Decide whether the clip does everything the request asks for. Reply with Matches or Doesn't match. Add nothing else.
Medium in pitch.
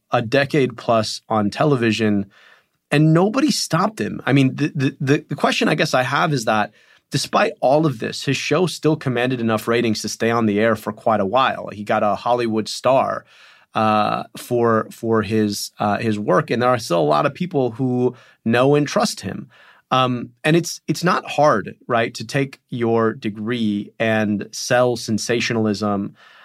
Doesn't match